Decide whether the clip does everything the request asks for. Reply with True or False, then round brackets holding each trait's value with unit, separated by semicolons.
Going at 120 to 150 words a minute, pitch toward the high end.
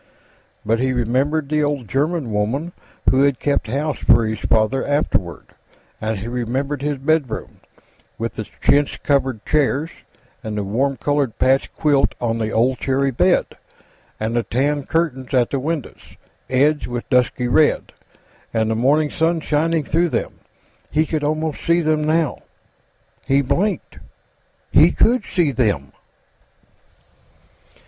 False (140 wpm; 135 Hz)